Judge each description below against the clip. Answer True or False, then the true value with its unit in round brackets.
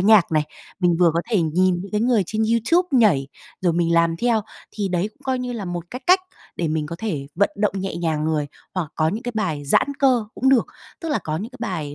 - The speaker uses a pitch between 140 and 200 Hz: True (185 Hz)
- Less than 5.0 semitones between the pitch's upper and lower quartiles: False (5.5 semitones)